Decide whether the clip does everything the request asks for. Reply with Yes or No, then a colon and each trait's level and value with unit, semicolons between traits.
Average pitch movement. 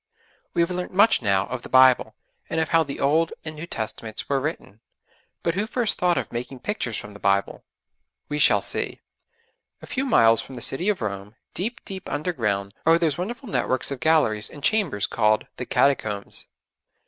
No: wide, 7.9 semitones